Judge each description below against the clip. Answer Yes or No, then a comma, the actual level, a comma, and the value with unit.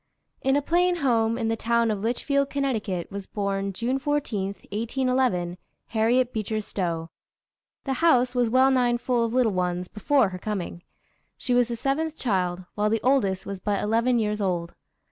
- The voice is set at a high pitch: Yes, high, 225 Hz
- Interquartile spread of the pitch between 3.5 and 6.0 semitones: Yes, average, 4.6 semitones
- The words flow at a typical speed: Yes, average, 175 wpm